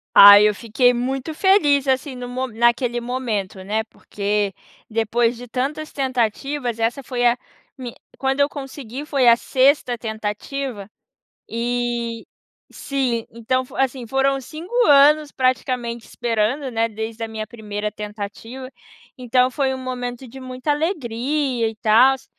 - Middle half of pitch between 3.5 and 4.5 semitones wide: No, average, 3.0 semitones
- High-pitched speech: Yes, high, 245 Hz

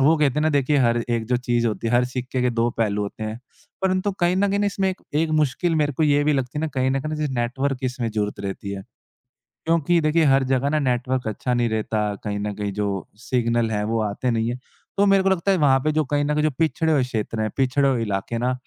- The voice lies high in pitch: No, low, 130 Hz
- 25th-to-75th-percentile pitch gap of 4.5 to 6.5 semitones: Yes, average, 4.8 semitones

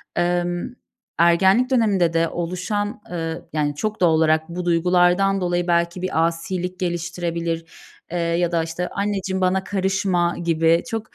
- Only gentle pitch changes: Yes, narrow, 2.1 semitones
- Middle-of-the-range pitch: Yes, medium, 175 Hz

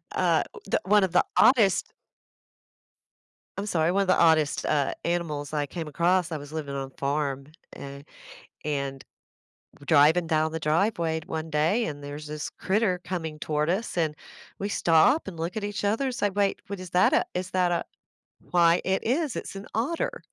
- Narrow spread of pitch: No, average, 4.3 semitones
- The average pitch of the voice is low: No, medium, 170 Hz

